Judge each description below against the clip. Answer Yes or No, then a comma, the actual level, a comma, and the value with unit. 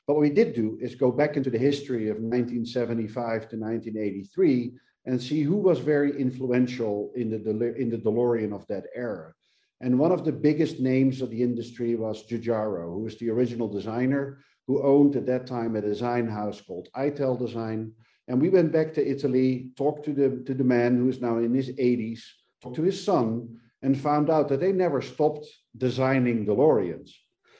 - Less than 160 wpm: No, average, 190 wpm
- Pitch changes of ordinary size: Yes, average, 3.2 semitones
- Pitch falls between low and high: No, low, 125 Hz